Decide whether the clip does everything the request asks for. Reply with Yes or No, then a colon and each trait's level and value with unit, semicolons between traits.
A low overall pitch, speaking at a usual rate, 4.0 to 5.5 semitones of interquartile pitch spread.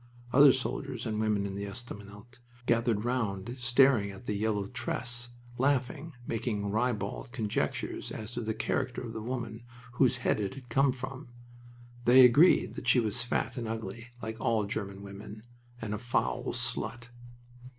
No: low, 115 Hz; average, 160 wpm; average, 2.9 semitones